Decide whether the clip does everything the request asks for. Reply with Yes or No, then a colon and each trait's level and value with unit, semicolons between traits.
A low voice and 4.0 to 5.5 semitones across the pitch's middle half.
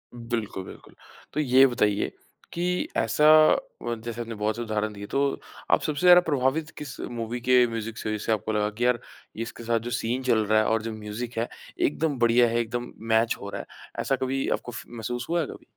No: low, 120 Hz; average, 2.8 semitones